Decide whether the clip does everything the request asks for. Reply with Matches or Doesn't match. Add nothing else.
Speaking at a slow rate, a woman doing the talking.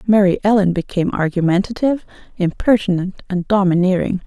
Matches